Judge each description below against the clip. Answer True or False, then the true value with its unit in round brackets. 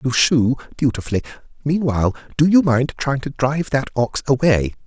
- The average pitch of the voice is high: False (135 Hz)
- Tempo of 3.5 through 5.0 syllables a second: False (5.4 syllables/s)